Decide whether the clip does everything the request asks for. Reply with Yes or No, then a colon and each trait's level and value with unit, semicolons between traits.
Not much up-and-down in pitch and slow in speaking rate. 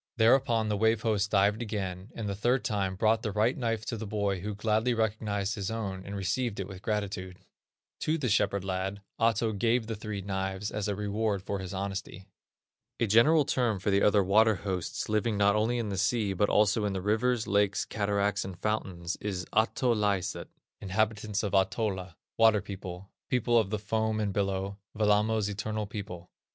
No: narrow, 2.1 semitones; average, 185 wpm